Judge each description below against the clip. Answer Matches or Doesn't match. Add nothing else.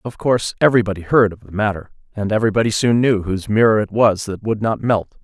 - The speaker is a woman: Doesn't match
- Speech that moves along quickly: Matches